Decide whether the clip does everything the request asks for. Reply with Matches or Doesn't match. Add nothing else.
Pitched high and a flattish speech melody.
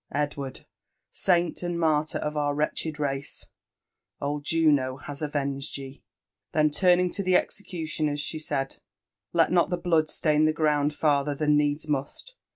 Doesn't match